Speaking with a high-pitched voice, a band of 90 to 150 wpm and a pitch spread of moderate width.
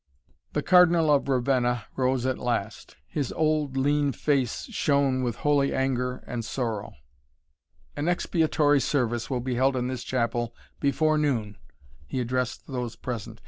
No: low, 130 Hz; average, 140 wpm; average, 3.1 semitones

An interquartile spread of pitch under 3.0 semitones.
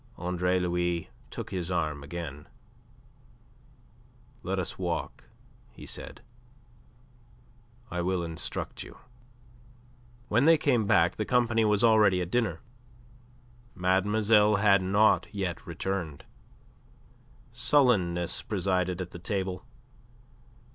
No: average, 3.4 semitones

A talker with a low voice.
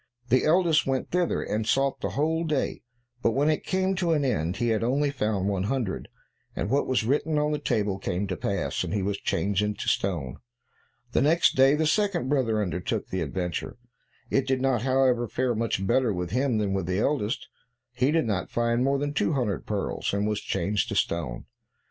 Yes: low, 120 Hz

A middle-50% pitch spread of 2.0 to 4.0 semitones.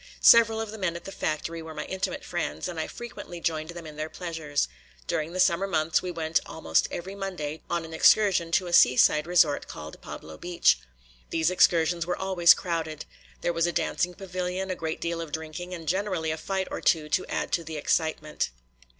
Yes: narrow, 2.5 semitones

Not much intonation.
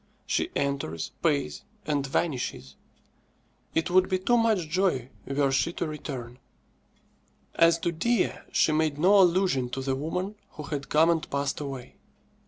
No: average, 4.5 semitones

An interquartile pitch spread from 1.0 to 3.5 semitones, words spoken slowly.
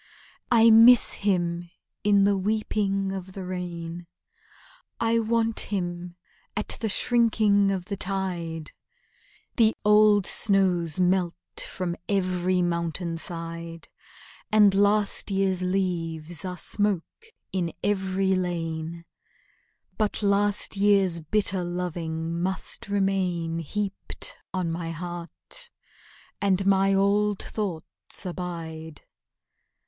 Yes: average, 2.9 semitones; slow, 100 wpm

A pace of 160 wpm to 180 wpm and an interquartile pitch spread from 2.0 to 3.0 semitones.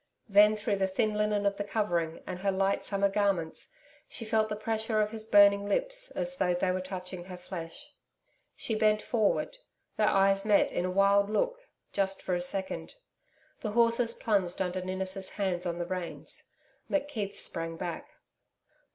Yes: average, 170 wpm; narrow, 2.6 semitones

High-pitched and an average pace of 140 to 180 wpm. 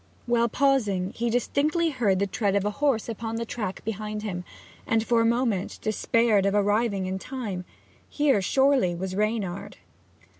Yes: high, 220 Hz; average, 160 wpm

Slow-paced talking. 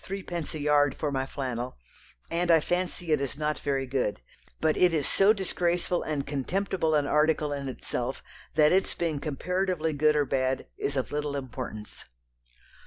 No: average, 175 wpm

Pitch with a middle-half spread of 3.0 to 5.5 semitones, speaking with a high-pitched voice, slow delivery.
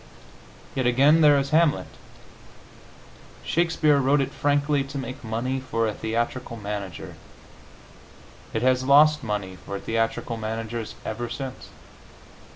No: average, 4.0 semitones; low, 130 Hz; slow, 120 wpm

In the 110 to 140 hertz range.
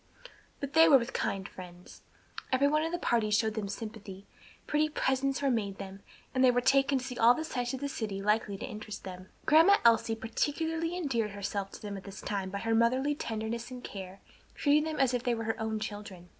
No: high, 230 Hz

